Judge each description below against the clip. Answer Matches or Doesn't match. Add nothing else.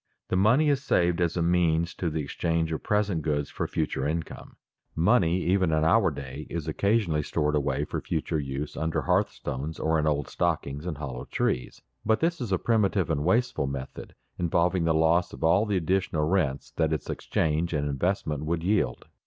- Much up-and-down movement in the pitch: Doesn't match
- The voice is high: Doesn't match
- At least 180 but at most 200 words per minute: Matches